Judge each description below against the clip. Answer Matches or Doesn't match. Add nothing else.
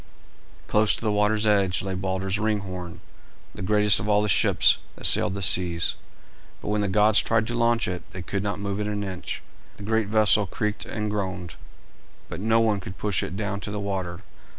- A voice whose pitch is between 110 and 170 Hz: Doesn't match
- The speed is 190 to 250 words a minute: Matches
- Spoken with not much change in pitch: Matches